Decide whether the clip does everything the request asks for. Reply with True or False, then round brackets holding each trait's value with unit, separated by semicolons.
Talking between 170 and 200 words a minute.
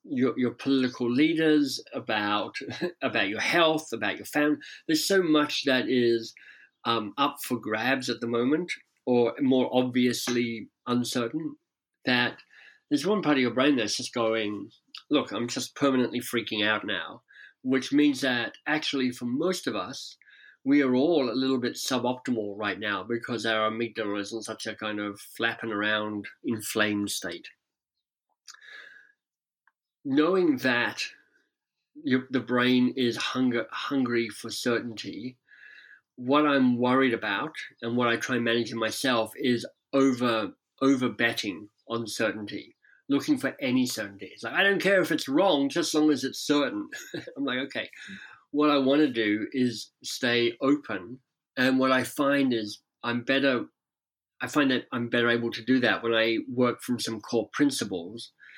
False (160 wpm)